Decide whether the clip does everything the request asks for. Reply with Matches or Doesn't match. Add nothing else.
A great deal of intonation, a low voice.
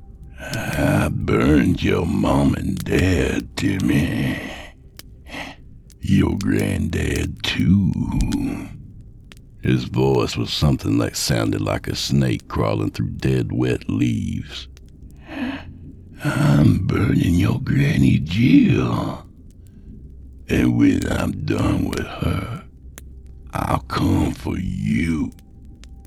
Matches